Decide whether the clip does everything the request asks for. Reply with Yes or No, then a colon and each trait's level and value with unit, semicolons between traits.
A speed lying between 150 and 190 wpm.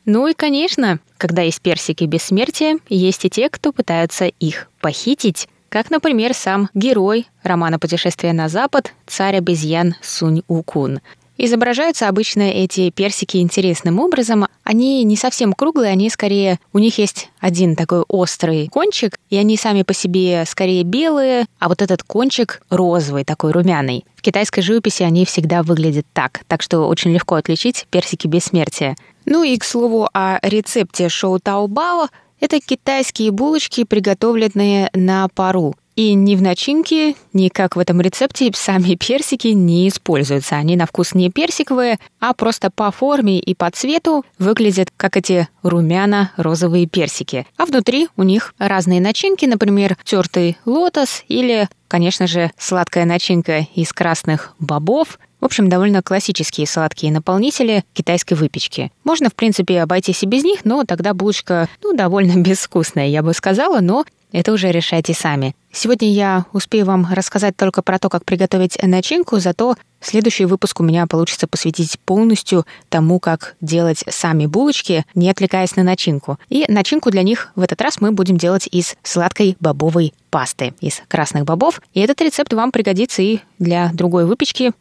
Yes: average, 155 wpm